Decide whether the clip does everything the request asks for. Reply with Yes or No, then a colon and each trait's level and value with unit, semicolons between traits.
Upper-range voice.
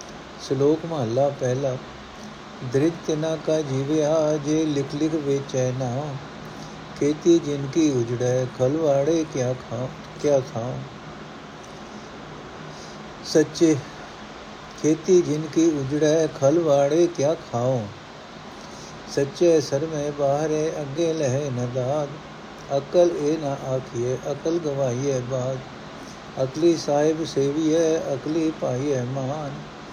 No: medium, 145 Hz